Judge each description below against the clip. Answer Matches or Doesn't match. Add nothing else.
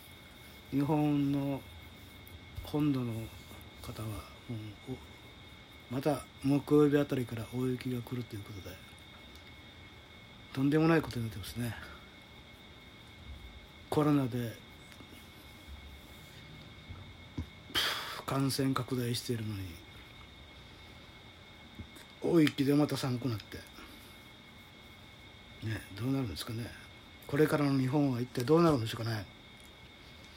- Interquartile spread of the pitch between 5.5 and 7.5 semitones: Doesn't match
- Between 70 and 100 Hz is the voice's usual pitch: Doesn't match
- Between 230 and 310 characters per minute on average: Doesn't match